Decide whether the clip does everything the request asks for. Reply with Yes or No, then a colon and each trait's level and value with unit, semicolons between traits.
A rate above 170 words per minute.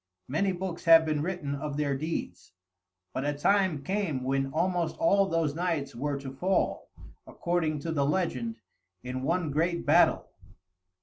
No: average, 150 wpm